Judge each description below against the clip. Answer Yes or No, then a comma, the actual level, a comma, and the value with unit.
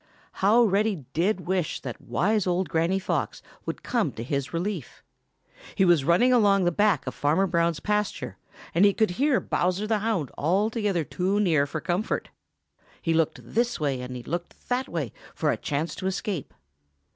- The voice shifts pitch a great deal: No, average, 4.5 semitones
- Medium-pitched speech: Yes, medium, 180 Hz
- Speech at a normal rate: Yes, average, 175 wpm